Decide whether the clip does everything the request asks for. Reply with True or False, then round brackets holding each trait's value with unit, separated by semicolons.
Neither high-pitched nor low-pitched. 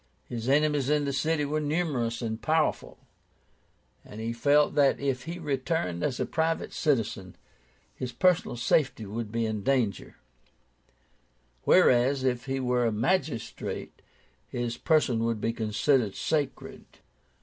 False (130 Hz)